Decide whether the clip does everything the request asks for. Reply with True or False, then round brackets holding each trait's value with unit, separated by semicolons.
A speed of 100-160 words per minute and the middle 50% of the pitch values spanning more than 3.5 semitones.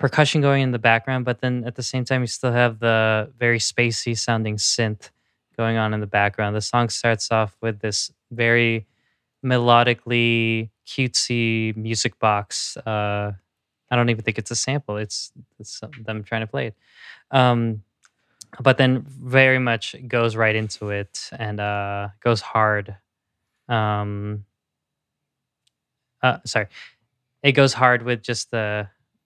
False (150 wpm; 2.6 semitones)